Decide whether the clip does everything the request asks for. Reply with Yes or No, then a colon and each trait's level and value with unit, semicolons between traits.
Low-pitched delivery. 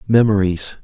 Yes: low, 105 Hz